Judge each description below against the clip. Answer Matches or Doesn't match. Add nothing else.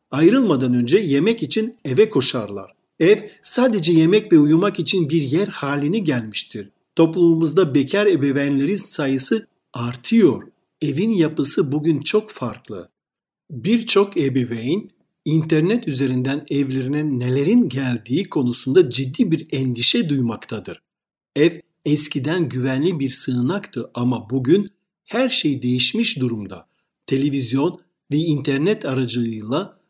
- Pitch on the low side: Doesn't match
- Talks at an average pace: Matches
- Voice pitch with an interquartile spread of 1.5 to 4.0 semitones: Doesn't match